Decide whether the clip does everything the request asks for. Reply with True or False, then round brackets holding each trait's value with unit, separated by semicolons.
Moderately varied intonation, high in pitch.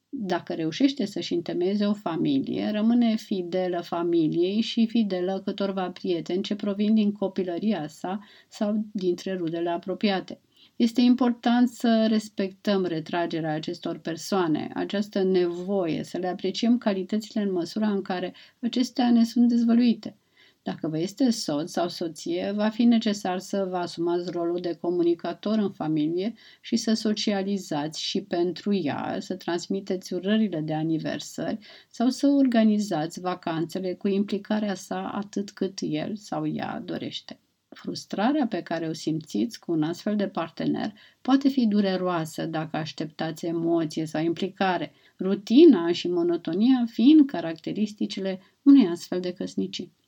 True (4.3 semitones; 195 Hz)